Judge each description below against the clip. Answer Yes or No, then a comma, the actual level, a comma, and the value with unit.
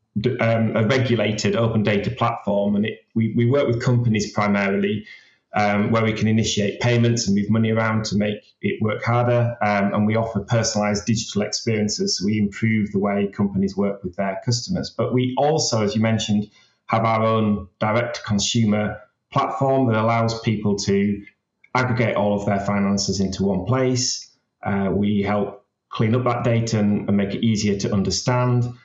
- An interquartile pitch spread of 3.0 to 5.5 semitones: No, narrow, 2.5 semitones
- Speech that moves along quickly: No, average, 175 wpm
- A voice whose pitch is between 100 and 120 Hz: Yes, low, 110 Hz